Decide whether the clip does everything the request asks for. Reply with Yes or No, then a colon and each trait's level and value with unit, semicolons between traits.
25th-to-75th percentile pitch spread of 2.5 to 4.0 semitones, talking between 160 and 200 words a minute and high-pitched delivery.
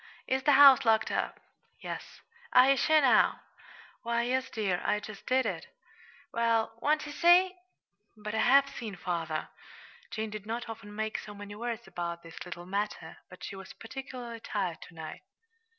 No: average, 4.7 semitones; average, 170 wpm; high, 225 Hz